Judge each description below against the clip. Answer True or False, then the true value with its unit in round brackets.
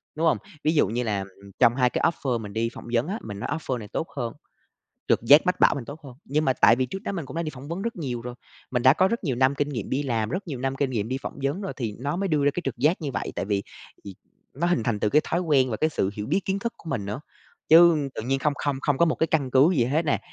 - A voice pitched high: False (135 Hz)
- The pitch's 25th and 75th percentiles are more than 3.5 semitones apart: True (5.0 semitones)